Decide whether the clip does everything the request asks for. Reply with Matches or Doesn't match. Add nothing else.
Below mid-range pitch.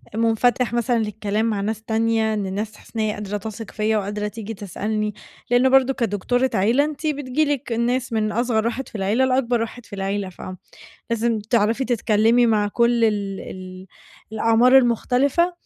Doesn't match